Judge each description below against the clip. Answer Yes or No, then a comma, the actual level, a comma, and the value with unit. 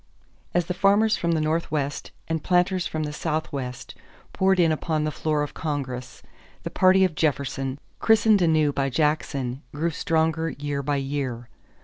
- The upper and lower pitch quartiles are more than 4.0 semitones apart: No, average, 3.2 semitones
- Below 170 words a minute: Yes, average, 155 wpm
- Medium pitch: Yes, medium, 155 Hz